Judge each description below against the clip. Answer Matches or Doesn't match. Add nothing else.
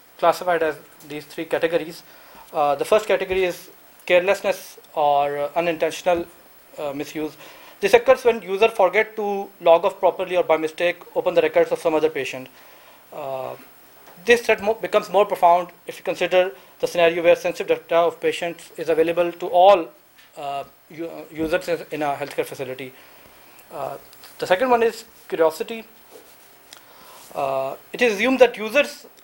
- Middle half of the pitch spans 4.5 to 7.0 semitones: Matches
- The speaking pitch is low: Doesn't match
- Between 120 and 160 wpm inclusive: Matches